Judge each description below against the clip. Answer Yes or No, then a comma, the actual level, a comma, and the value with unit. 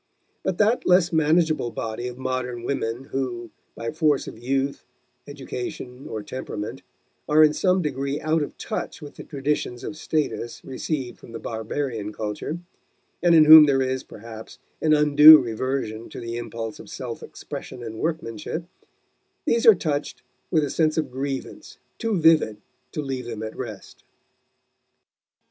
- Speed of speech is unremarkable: Yes, average, 155 wpm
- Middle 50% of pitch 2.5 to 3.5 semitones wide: No, average, 4.7 semitones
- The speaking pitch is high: No, low, 135 Hz